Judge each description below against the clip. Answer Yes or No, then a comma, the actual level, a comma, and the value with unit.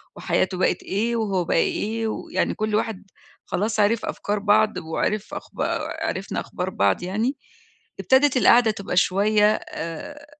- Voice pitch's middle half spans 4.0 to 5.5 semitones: No, average, 3.2 semitones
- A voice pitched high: Yes, high, 210 Hz